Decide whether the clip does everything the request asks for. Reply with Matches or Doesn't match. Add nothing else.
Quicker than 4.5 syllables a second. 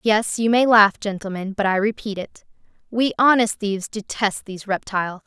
Matches